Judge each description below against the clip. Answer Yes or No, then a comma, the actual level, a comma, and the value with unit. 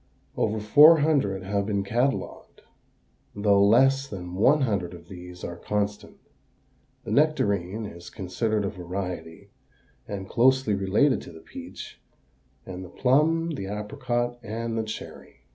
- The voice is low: Yes, low, 105 Hz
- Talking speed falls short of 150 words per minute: Yes, slow, 135 wpm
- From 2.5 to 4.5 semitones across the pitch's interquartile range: No, average, 5.1 semitones